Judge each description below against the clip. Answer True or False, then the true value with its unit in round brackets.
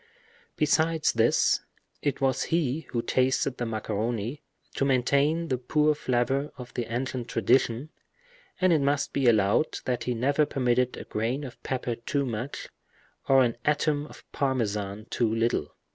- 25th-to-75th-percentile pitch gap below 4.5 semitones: True (3.4 semitones)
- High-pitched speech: False (130 Hz)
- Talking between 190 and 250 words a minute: False (150 wpm)